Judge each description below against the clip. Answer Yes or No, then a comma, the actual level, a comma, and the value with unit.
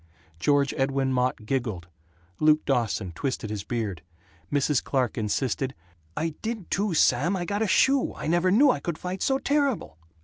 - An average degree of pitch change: No, wide, 7.3 semitones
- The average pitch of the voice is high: No, medium, 140 Hz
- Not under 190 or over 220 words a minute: No, average, 165 wpm